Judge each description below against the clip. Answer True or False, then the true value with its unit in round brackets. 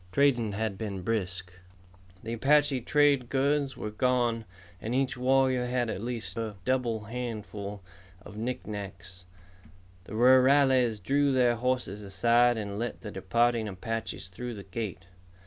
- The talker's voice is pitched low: True (115 Hz)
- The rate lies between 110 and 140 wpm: True (135 wpm)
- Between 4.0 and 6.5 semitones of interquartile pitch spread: False (3.5 semitones)